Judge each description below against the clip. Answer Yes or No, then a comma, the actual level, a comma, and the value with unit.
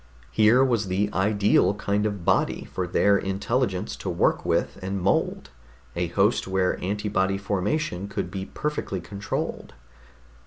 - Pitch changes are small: Yes, narrow, 1.7 semitones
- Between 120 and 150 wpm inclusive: Yes, average, 140 wpm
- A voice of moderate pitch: No, low, 100 Hz